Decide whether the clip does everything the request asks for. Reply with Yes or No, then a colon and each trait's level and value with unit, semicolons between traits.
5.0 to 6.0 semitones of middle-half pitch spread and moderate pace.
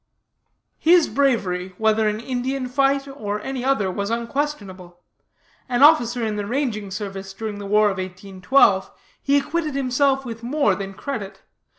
Yes: wide, 5.4 semitones; average, 150 wpm